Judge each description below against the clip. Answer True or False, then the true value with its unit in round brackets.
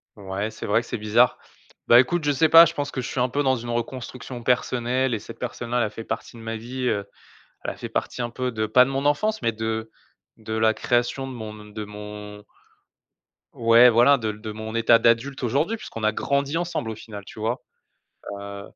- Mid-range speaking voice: False (115 Hz)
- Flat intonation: False (3.0 semitones)